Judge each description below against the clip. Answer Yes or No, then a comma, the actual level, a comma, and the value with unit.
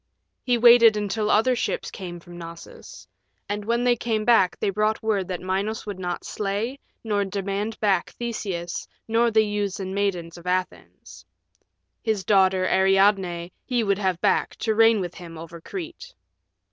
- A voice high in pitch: Yes, high, 200 Hz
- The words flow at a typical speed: Yes, average, 160 wpm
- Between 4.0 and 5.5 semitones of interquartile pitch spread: No, average, 3.1 semitones